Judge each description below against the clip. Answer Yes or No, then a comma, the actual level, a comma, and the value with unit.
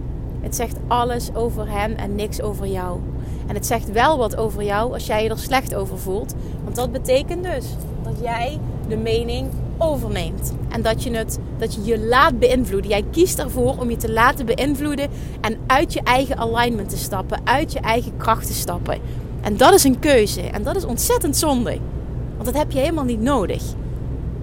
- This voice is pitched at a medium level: No, high, 245 Hz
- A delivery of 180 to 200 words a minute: Yes, average, 195 wpm